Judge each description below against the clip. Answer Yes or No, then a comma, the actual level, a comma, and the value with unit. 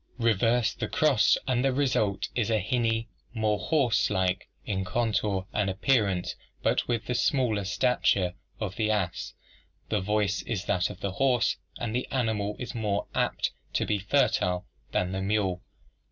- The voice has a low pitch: Yes, low, 105 Hz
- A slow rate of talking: No, average, 155 wpm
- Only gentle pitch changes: No, average, 3.7 semitones